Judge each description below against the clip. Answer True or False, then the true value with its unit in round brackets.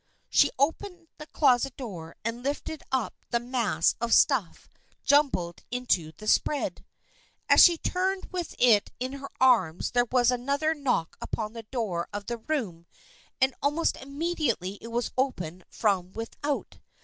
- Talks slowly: False (150 wpm)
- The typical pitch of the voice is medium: False (245 Hz)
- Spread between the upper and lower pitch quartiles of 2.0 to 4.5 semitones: False (5.1 semitones)